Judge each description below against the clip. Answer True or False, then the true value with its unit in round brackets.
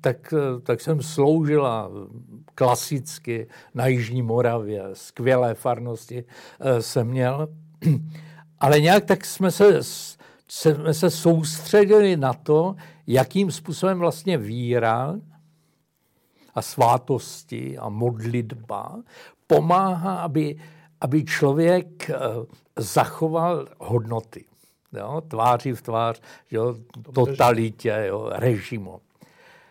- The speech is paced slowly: True (85 wpm)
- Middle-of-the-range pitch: True (145 Hz)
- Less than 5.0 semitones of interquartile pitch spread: False (5.5 semitones)